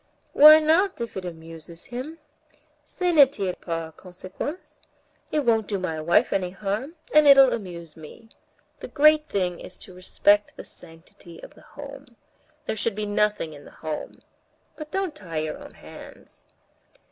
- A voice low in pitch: No, high, 205 Hz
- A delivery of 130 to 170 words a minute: Yes, average, 165 wpm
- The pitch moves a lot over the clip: Yes, wide, 8.8 semitones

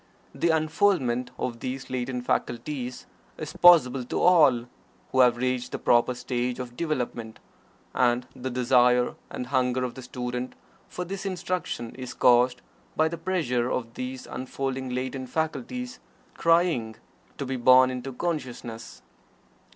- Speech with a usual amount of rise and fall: Yes, average, 3.6 semitones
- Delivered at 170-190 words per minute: No, slow, 135 wpm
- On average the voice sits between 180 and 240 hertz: No, low, 130 Hz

